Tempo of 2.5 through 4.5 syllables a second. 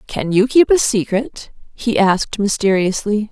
Yes: 4.4 syllables/s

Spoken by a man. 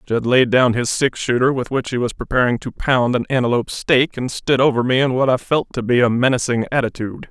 Yes: male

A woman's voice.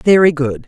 Yes: female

